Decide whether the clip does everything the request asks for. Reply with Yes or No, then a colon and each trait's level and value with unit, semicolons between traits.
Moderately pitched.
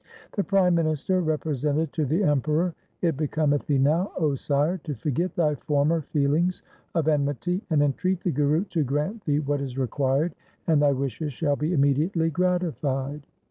Yes: medium, 150 Hz